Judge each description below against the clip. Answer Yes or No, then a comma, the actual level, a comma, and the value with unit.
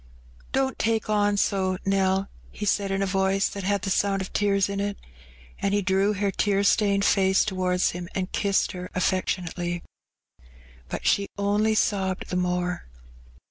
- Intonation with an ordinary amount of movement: No, narrow, 1.4 semitones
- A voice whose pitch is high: Yes, high, 195 Hz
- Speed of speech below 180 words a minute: Yes, average, 170 wpm